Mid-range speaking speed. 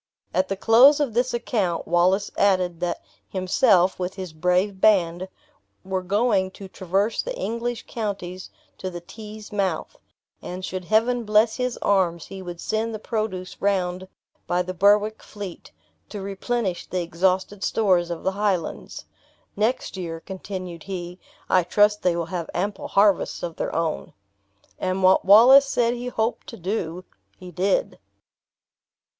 Yes: average, 150 wpm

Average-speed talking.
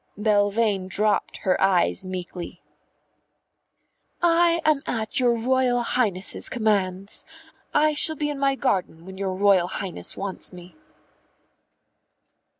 No: slow, 115 wpm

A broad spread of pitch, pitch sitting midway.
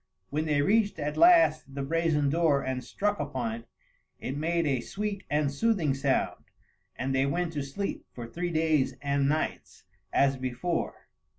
No: average, 3.8 semitones; medium, 150 Hz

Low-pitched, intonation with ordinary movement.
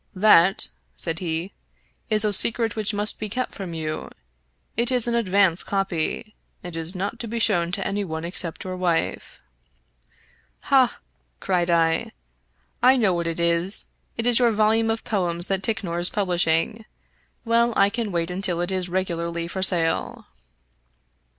No: high, 190 Hz; average, 4.2 semitones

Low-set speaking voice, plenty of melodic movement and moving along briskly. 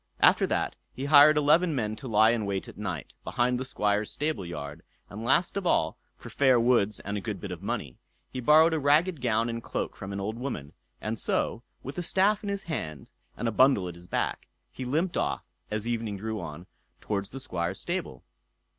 Yes: low, 115 Hz; wide, 6.2 semitones; fast, 210 wpm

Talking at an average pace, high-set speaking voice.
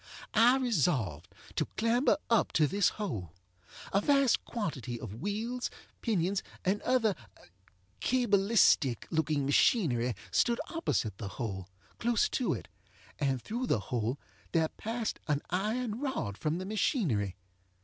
No: slow, 130 wpm; high, 195 Hz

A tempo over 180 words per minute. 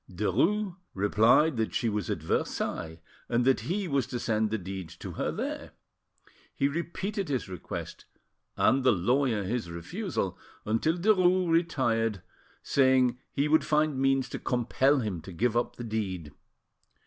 No: average, 150 wpm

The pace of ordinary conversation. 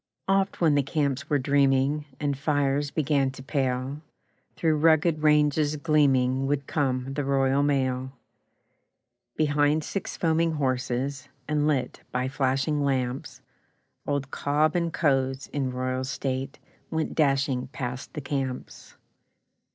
No: slow, 125 wpm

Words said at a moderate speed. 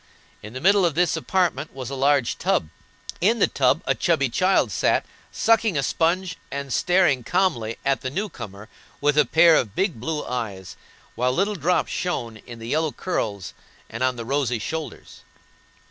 Yes: average, 175 wpm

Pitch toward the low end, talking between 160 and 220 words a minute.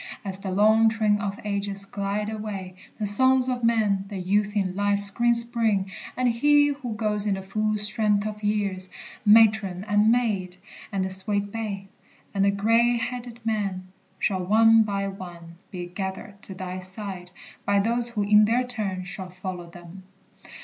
No: high, 205 Hz; average, 170 wpm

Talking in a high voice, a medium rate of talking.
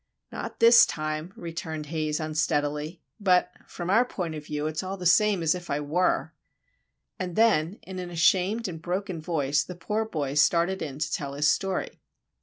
No: medium, 170 Hz; average, 180 wpm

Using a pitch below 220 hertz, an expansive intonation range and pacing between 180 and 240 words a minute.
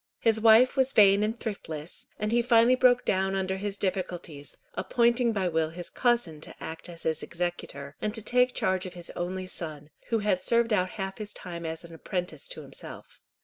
No: high, 190 Hz; average, 5.0 semitones; average, 190 wpm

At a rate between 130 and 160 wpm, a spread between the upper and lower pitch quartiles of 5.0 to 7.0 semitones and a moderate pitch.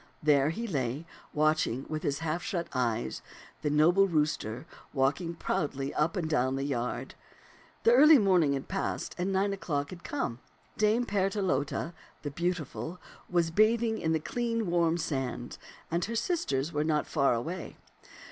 Yes: average, 155 wpm; average, 5.3 semitones; medium, 160 Hz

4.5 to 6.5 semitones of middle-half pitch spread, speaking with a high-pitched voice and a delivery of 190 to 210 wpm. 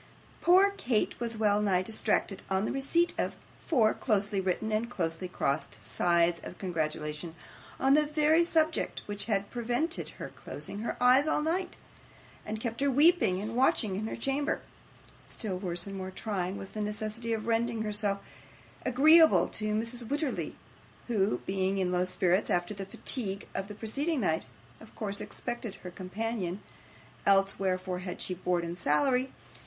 No: average, 4.8 semitones; high, 210 Hz; average, 160 wpm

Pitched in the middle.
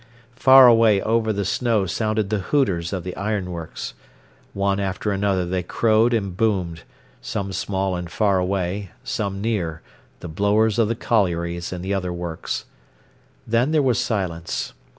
No: low, 100 Hz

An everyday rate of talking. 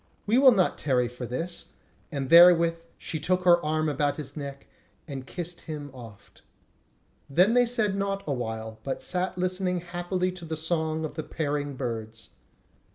Yes: average, 160 wpm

